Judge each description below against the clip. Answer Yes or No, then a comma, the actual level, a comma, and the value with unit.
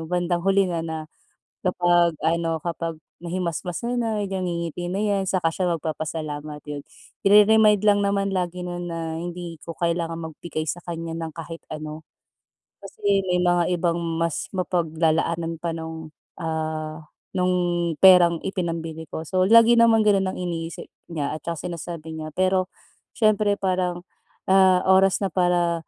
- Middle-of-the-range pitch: Yes, medium, 175 Hz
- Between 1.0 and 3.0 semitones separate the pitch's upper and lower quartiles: Yes, narrow, 2.5 semitones